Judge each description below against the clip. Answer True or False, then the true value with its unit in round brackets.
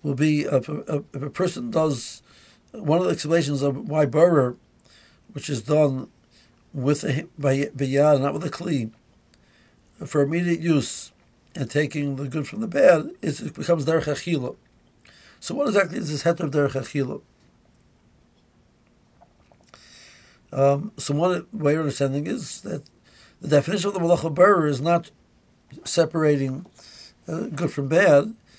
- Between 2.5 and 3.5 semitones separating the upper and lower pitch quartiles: True (3.2 semitones)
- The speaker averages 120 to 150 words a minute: True (145 wpm)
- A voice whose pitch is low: False (145 Hz)